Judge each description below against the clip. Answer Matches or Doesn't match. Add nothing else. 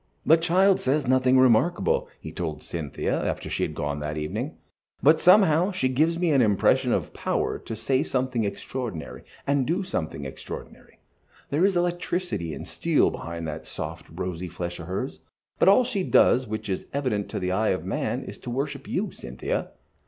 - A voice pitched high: Doesn't match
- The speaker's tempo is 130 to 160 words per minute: Doesn't match